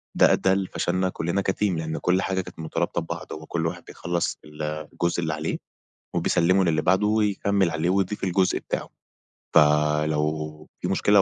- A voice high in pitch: No, very low, 85 Hz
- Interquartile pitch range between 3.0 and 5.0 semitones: Yes, average, 3.5 semitones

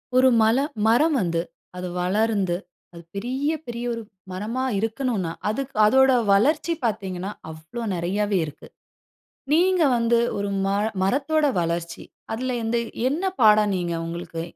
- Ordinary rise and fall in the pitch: No, wide, 5.7 semitones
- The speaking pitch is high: Yes, high, 215 Hz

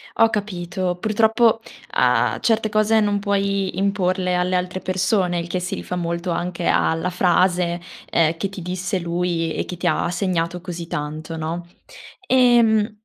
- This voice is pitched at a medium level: Yes, medium, 180 Hz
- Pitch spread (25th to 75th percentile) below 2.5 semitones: No, average, 2.8 semitones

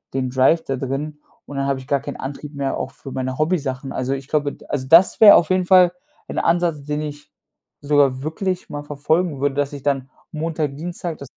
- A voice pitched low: No, medium, 145 Hz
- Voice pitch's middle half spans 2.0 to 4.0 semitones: Yes, average, 2.9 semitones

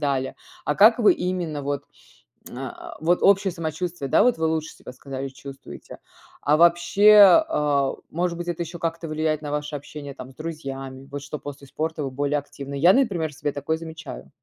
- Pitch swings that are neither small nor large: Yes, average, 3.3 semitones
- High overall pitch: No, medium, 155 Hz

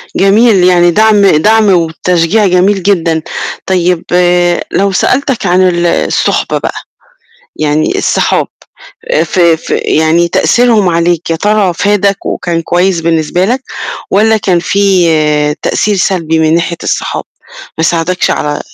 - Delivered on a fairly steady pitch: No, average, 3.3 semitones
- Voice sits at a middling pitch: Yes, medium, 180 Hz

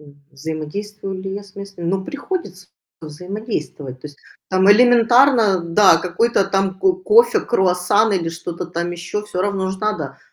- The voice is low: No, high, 190 Hz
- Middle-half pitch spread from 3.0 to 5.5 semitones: Yes, average, 3.4 semitones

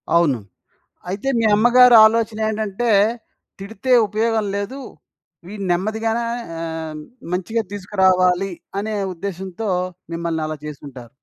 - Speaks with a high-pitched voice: Yes, high, 200 Hz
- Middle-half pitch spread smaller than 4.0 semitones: No, average, 4.5 semitones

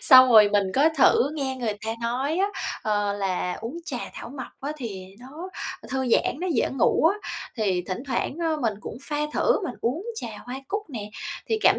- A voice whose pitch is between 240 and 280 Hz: Yes, very high, 255 Hz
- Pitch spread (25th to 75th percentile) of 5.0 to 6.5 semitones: Yes, wide, 5.5 semitones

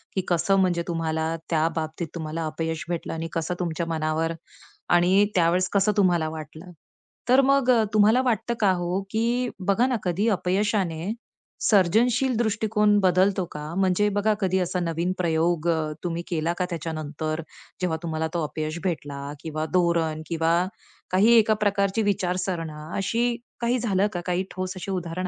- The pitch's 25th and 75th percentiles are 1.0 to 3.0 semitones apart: No, average, 3.7 semitones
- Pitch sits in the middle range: Yes, medium, 180 Hz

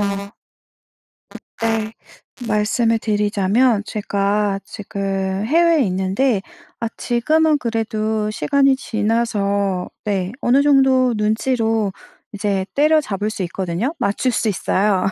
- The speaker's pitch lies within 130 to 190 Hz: No, high, 215 Hz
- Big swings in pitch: No, average, 3.4 semitones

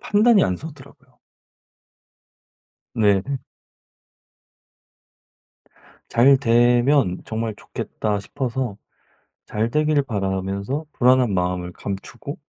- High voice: No, low, 120 Hz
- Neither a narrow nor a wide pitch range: No, wide, 5.7 semitones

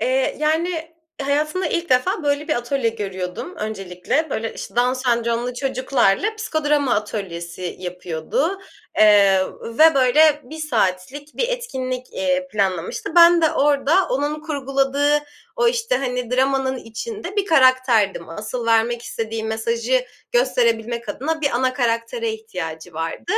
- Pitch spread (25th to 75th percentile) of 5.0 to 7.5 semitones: Yes, average, 5.3 semitones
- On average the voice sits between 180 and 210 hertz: No, very high, 255 Hz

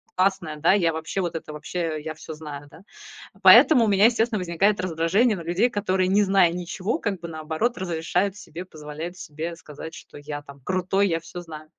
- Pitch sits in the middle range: Yes, medium, 175 Hz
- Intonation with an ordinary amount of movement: Yes, average, 3.5 semitones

